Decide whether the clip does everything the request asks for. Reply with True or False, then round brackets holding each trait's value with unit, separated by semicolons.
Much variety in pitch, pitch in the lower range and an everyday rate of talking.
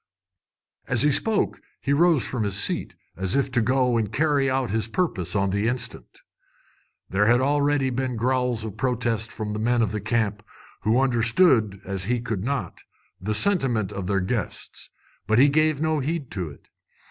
False (4.2 semitones; 120 Hz; 180 wpm)